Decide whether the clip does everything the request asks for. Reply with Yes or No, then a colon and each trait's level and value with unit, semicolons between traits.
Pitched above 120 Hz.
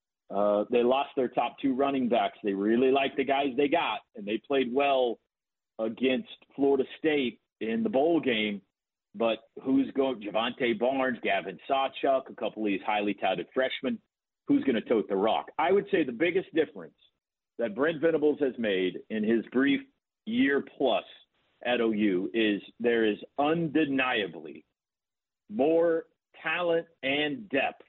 Yes: low, 135 Hz